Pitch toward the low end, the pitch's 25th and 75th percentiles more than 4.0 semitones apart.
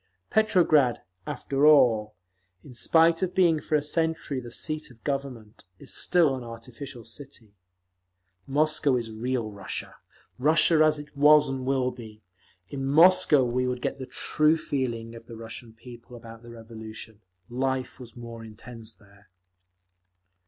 Yes: low, 125 Hz; average, 4.5 semitones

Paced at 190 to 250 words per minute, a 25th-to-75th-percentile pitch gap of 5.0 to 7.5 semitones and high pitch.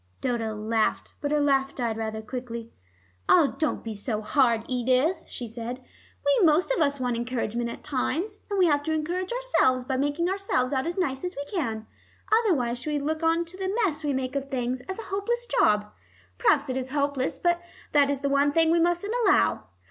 Yes: average, 200 wpm; average, 5.3 semitones; very high, 280 Hz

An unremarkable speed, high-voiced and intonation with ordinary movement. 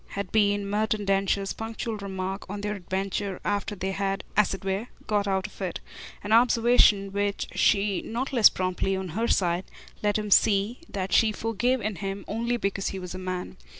No: average, 185 wpm; high, 200 Hz; narrow, 1.8 semitones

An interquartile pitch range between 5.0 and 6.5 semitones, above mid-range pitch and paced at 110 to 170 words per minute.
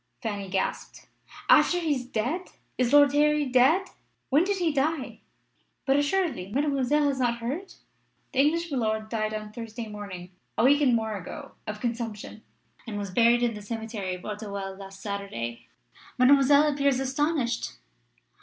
Yes: average, 5.3 semitones; high, 240 Hz; average, 155 wpm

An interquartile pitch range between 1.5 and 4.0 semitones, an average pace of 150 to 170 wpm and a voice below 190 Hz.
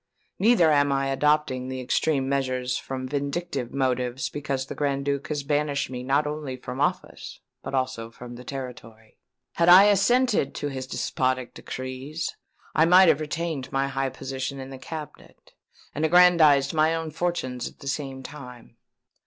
Yes: average, 2.9 semitones; average, 160 wpm; medium, 140 Hz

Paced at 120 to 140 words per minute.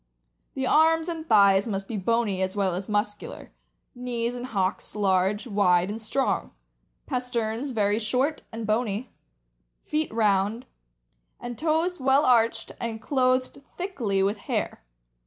Yes: slow, 135 wpm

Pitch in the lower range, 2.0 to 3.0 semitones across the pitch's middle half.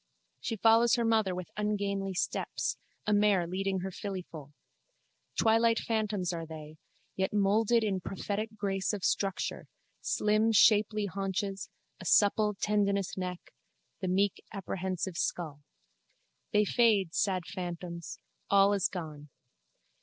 No: high, 195 Hz; narrow, 2.5 semitones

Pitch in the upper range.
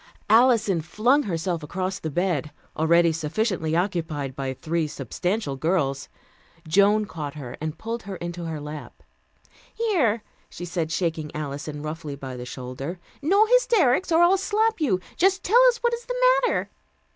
No: medium, 175 Hz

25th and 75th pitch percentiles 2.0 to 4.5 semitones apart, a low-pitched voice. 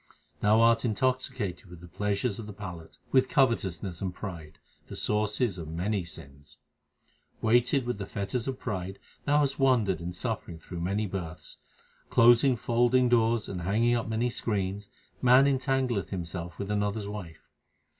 No: average, 4.9 semitones; low, 105 Hz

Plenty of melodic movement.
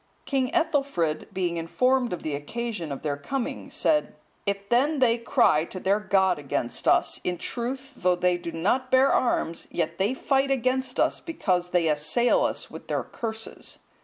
Yes: wide, 7.3 semitones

